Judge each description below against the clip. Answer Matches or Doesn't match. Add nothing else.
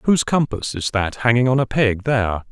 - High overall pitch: Doesn't match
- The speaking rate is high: Matches